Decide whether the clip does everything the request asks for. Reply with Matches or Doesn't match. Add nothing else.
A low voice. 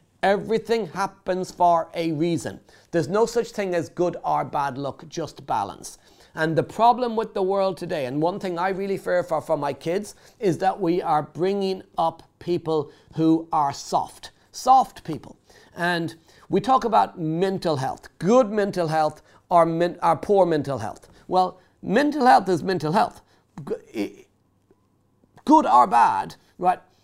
Doesn't match